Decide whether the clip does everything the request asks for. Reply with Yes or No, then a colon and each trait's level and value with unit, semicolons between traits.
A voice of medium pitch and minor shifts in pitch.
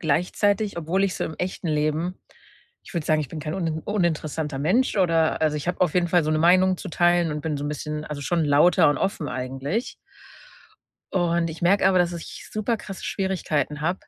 No: medium, 170 Hz; average, 3.3 semitones